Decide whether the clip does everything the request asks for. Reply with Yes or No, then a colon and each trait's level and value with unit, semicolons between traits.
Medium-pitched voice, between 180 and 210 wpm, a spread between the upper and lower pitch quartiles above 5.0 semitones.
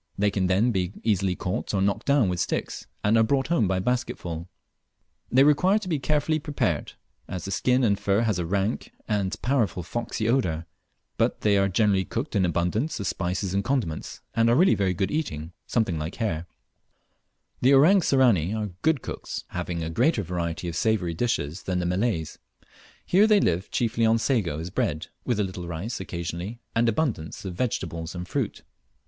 No: low, 100 Hz; average, 190 wpm; wide, 5.6 semitones